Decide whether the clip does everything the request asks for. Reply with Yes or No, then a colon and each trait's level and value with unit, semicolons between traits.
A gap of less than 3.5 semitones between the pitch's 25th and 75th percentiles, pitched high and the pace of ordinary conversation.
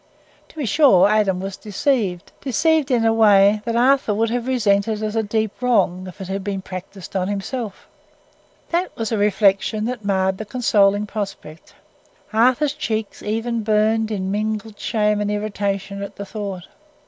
Yes: narrow, 2.4 semitones; high, 210 Hz; average, 160 wpm